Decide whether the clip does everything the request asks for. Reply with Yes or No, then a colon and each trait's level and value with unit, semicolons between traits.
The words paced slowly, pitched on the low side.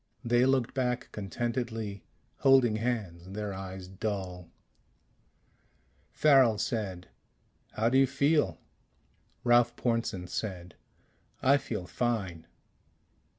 Yes: slow, 95 wpm; low, 110 Hz